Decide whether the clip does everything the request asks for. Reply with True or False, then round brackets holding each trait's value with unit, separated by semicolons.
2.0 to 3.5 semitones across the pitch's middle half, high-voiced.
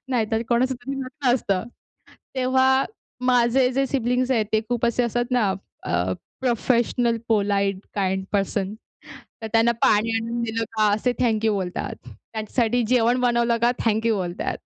True (2.6 semitones; 235 Hz)